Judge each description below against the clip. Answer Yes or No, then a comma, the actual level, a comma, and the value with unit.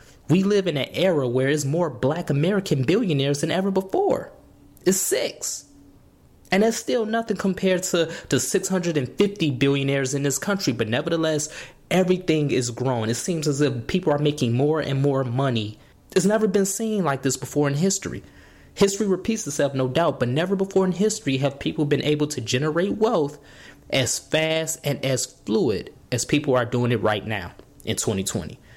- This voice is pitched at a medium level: Yes, medium, 150 Hz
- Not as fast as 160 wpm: No, average, 175 wpm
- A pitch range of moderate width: No, wide, 6.1 semitones